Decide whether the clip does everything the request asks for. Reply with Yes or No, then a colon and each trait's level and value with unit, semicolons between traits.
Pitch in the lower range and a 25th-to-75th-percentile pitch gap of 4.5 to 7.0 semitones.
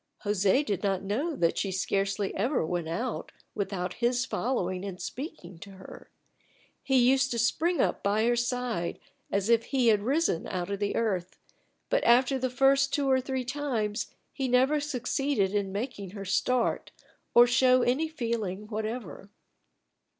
No: high, 235 Hz; average, 4.8 semitones